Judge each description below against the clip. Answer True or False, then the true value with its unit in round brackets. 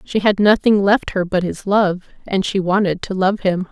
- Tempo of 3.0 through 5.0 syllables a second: True (4.7 syllables/s)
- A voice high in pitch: True (195 Hz)